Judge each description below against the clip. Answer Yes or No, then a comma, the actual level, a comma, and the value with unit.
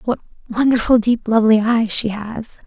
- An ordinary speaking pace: Yes, average, 160 wpm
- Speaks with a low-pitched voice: No, high, 225 Hz